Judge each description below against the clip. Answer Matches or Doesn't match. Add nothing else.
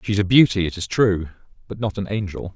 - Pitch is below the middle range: Matches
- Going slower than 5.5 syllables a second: Doesn't match